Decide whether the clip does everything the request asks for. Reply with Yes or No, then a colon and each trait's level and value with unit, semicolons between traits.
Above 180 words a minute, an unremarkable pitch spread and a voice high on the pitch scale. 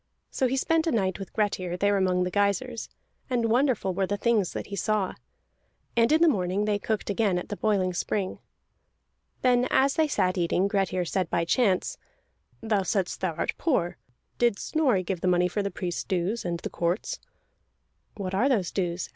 Yes: average, 190 wpm; average, 4.2 semitones; high, 200 Hz